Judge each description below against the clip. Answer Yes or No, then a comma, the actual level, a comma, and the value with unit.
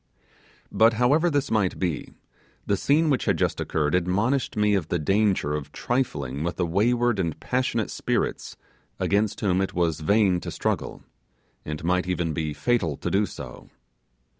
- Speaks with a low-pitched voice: Yes, very low, 95 Hz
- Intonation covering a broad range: Yes, wide, 5.9 semitones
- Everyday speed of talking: Yes, average, 165 wpm